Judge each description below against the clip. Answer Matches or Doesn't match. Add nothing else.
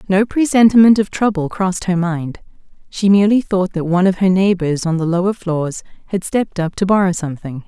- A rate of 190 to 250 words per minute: Matches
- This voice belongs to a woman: Matches